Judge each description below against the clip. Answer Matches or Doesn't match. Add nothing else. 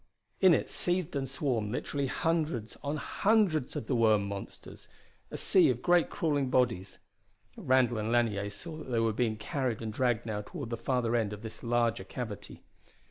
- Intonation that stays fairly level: Doesn't match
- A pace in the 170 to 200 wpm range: Matches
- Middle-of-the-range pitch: Doesn't match